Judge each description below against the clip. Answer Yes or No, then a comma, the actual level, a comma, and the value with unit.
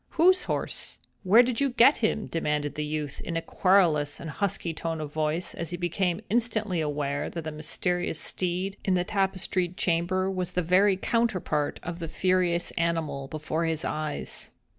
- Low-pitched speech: No, medium, 175 Hz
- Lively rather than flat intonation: No, average, 3.6 semitones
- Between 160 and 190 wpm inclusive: Yes, average, 170 wpm